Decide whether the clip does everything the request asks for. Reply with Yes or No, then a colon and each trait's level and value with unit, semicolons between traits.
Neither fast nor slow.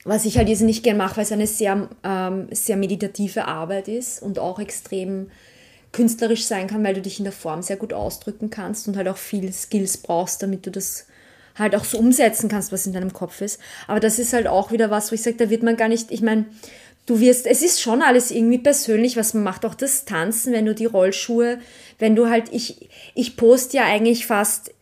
No: fast, 230 wpm